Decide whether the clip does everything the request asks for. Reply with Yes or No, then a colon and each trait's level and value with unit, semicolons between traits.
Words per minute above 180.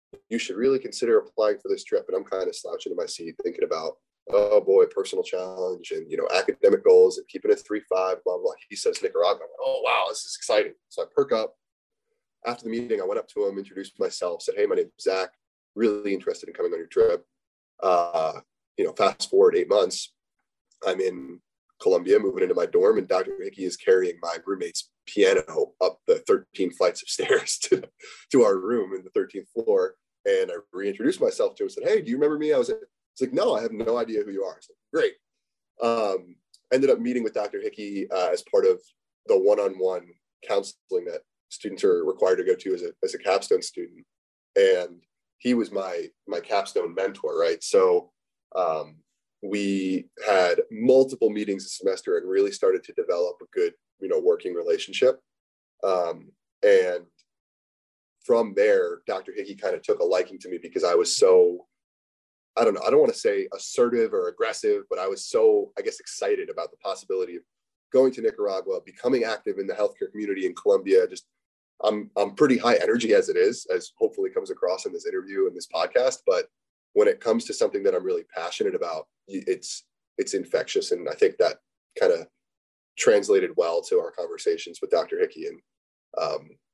Yes: average, 200 wpm